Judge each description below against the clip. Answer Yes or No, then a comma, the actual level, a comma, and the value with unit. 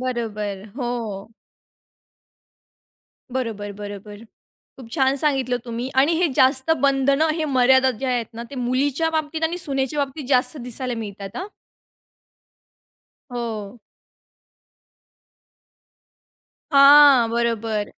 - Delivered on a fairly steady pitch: No, average, 3.5 semitones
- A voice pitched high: Yes, very high, 255 Hz